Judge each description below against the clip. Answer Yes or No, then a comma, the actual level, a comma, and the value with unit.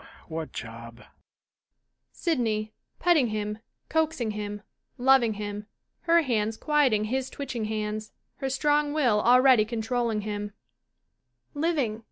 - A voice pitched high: Yes, high, 225 Hz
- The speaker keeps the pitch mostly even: No, average, 4.2 semitones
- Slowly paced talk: Yes, slow, 125 wpm